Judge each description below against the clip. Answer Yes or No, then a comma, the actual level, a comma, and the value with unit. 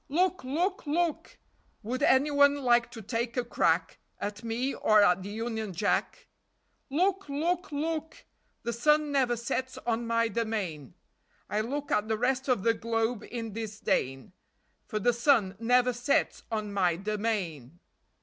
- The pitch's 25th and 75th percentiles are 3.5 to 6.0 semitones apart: Yes, average, 4.6 semitones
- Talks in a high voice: Yes, high, 235 Hz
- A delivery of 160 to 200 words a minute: No, average, 150 wpm